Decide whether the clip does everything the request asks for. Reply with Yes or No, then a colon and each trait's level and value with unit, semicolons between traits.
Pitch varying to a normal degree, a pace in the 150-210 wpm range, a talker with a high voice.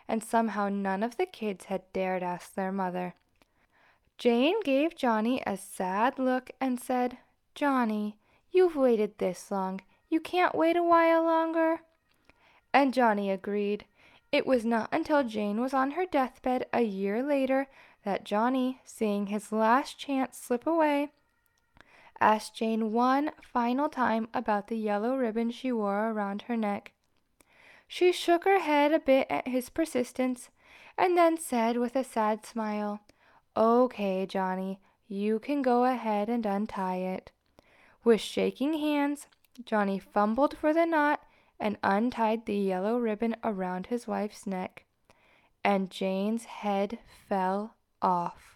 No: average, 4.8 semitones; average, 140 wpm; high, 235 Hz